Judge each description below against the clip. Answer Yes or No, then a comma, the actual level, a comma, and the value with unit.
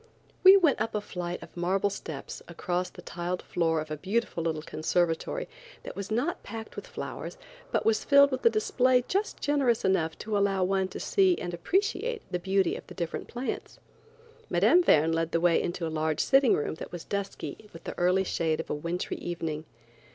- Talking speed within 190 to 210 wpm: Yes, average, 195 wpm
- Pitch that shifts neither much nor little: No, wide, 5.9 semitones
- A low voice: No, high, 190 Hz